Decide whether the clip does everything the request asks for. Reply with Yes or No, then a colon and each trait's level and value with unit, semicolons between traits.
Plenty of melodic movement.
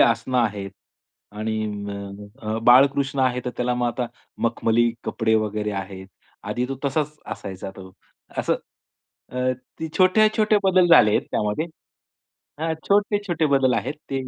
Yes: wide, 6.0 semitones